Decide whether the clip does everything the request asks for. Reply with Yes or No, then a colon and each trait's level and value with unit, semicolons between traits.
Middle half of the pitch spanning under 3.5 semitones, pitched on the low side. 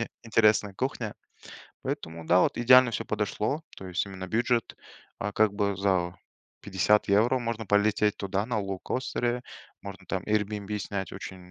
Yes: average, 2.8 semitones; low, 105 Hz